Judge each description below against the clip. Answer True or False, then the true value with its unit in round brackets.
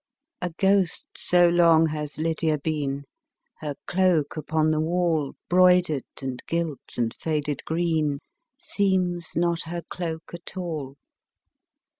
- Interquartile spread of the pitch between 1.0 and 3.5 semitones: True (2.5 semitones)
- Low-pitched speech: False (165 Hz)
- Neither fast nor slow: False (120 wpm)